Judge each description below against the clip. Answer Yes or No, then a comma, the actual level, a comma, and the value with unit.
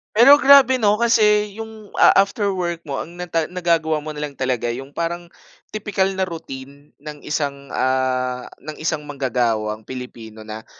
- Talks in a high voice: No, medium, 155 Hz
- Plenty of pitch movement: Yes, wide, 6.8 semitones